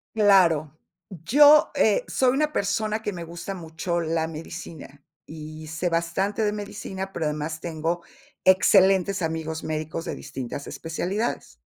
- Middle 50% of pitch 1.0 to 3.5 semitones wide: No, average, 4.0 semitones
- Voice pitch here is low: No, medium, 170 Hz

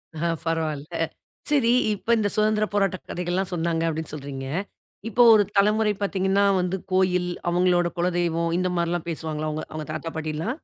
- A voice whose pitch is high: No, medium, 175 Hz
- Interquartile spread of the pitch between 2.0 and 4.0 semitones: Yes, average, 3.5 semitones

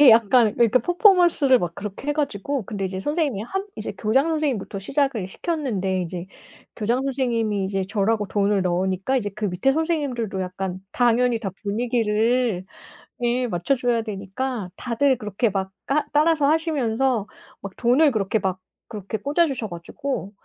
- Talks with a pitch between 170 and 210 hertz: No, high, 230 Hz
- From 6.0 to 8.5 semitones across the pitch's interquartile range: No, wide, 5.5 semitones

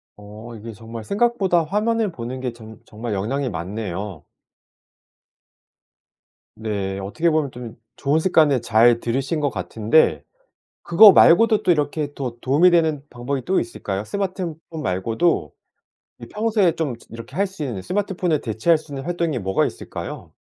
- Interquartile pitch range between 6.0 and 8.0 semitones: Yes, wide, 7.2 semitones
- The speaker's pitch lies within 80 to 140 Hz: Yes, low, 135 Hz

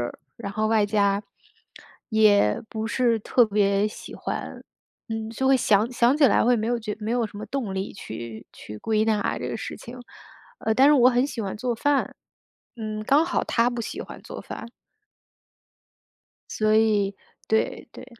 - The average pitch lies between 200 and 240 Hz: Yes, high, 220 Hz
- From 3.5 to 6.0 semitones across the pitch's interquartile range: No, average, 2.7 semitones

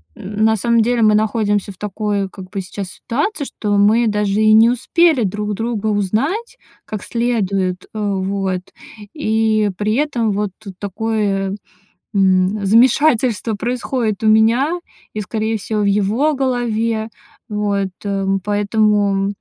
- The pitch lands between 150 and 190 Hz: No, high, 215 Hz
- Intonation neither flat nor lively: No, narrow, 2.3 semitones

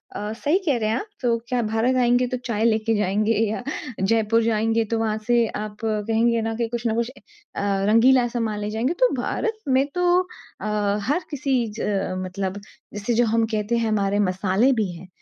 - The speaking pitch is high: Yes, high, 225 Hz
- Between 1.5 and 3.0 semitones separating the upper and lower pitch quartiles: Yes, narrow, 2.4 semitones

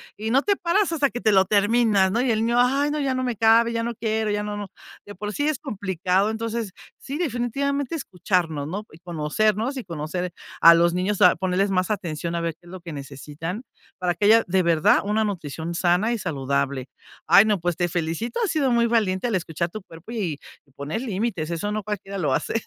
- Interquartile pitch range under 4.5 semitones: No, average, 5.0 semitones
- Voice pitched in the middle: No, high, 205 Hz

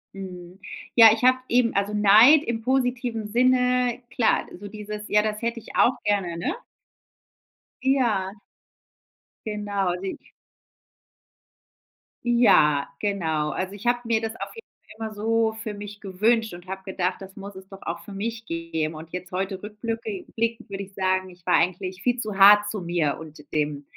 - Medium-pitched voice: No, high, 205 Hz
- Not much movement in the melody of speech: No, average, 3.5 semitones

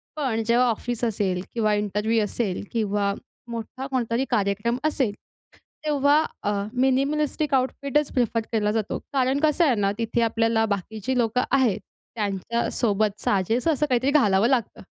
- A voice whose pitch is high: Yes, high, 235 Hz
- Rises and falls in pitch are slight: No, average, 4.0 semitones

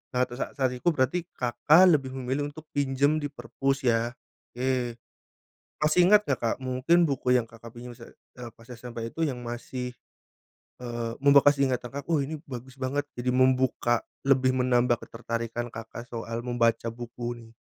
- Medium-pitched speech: No, low, 125 Hz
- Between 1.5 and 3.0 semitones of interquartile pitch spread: Yes, narrow, 2.4 semitones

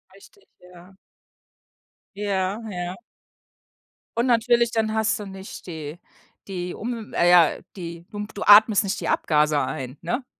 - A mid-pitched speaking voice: No, high, 195 Hz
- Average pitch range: Yes, average, 3.9 semitones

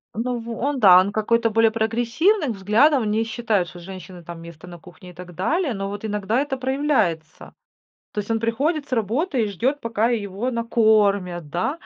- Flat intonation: No, average, 4.5 semitones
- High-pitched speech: Yes, high, 220 Hz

